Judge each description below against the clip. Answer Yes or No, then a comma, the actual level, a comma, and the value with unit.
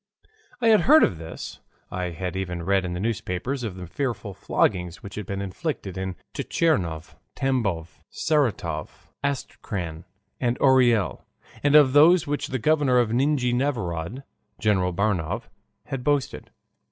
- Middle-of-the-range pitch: No, low, 110 Hz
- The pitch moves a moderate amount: No, wide, 7.1 semitones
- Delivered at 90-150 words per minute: Yes, average, 145 wpm